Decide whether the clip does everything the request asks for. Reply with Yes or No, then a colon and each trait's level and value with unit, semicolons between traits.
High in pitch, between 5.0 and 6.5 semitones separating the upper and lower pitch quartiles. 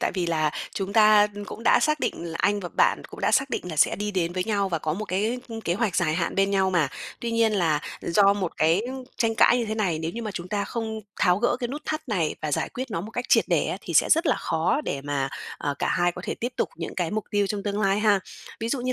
No: high, 200 Hz; average, 4.6 semitones